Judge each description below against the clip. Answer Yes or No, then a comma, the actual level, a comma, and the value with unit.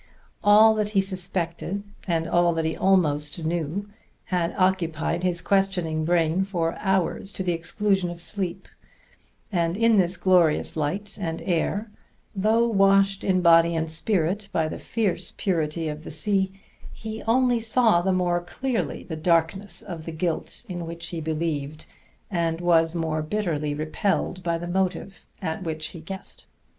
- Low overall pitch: No, medium, 175 Hz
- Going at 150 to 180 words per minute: Yes, average, 155 wpm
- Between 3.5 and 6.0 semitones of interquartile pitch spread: No, average, 3.1 semitones